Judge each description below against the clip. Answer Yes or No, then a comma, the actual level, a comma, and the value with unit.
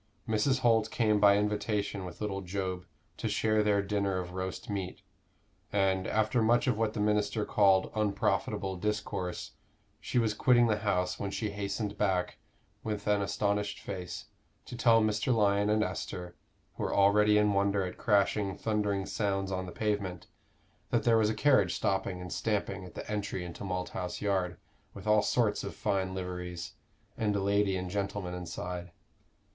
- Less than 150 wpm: No, average, 165 wpm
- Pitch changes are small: Yes, narrow, 2.1 semitones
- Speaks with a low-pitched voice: Yes, low, 100 Hz